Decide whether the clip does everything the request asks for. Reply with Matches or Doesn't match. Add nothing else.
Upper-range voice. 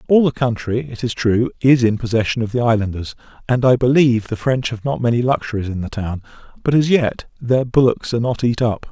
Doesn't match